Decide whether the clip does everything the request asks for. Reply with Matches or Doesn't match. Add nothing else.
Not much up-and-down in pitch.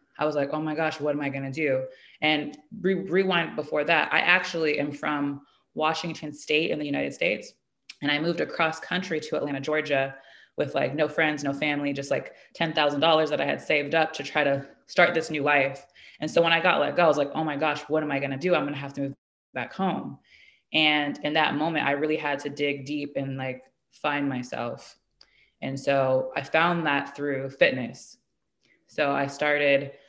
Matches